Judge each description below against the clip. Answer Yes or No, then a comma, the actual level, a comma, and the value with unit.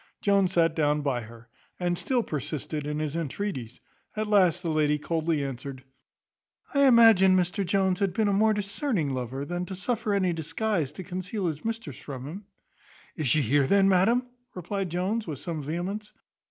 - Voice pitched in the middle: Yes, medium, 175 Hz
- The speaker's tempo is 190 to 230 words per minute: No, average, 175 wpm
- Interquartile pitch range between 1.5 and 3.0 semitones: No, average, 5.2 semitones